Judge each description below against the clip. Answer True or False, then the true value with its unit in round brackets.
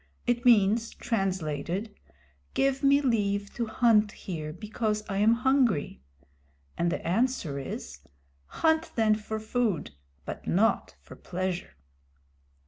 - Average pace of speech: False (120 wpm)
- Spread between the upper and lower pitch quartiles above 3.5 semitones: True (4.2 semitones)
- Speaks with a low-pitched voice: False (215 Hz)